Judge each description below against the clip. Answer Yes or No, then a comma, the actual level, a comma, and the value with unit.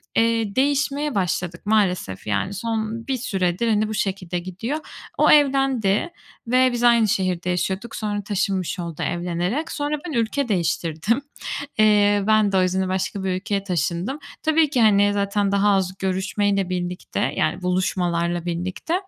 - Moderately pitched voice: No, high, 200 Hz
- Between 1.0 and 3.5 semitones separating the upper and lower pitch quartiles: No, average, 4.0 semitones